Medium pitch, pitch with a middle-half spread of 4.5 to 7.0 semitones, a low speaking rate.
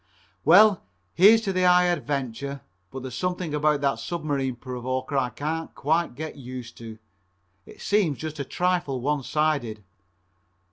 No: medium, 145 Hz; average, 4.9 semitones; average, 145 wpm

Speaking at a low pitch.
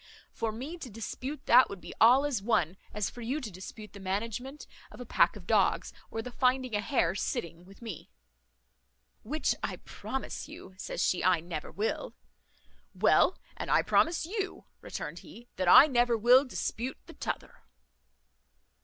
No: high, 230 Hz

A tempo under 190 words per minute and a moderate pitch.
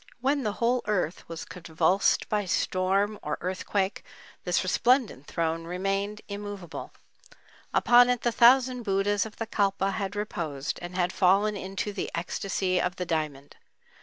No: average, 145 wpm; high, 195 Hz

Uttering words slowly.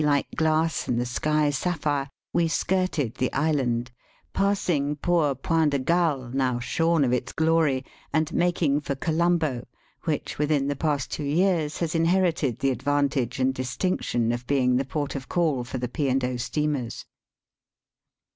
No: average, 155 wpm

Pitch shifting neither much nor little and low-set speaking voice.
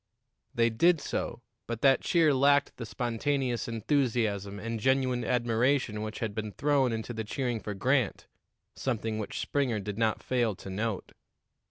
Yes: average, 3.4 semitones; low, 115 Hz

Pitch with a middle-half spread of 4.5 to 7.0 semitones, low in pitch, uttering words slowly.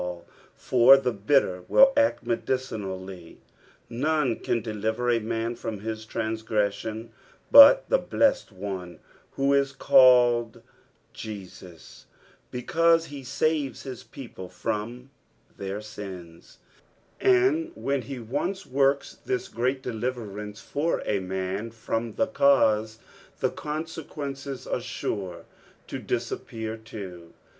Yes: average, 4.9 semitones; low, 115 Hz; slow, 115 wpm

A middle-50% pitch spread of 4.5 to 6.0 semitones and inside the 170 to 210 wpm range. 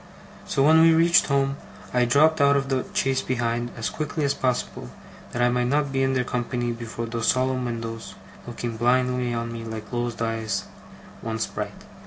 No: average, 2.7 semitones; average, 185 wpm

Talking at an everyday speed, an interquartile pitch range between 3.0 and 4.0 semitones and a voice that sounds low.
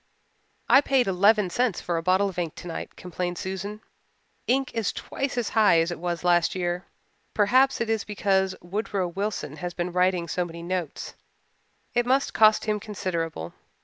No: average, 170 wpm; average, 3.6 semitones; medium, 185 Hz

